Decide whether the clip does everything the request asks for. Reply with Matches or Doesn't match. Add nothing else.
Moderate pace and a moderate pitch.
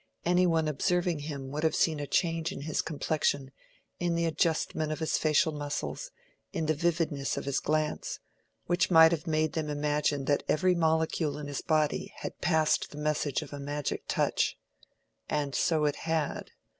Matches